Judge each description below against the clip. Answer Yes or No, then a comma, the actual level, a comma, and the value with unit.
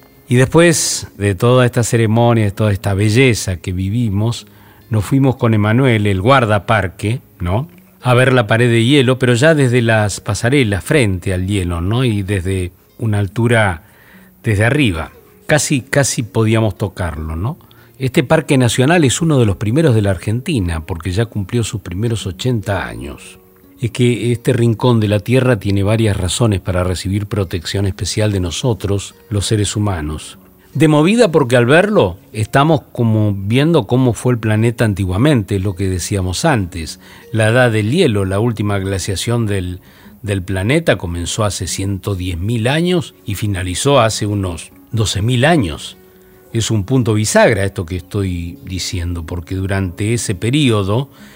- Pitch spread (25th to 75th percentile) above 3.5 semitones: Yes, average, 4.2 semitones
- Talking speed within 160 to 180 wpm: No, average, 150 wpm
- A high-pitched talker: No, low, 105 Hz